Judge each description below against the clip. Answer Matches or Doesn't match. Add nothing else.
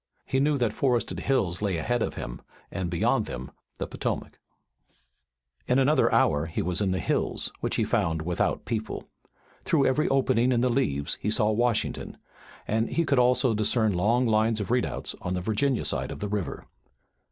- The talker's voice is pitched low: Matches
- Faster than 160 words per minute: Matches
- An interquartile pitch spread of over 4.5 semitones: Matches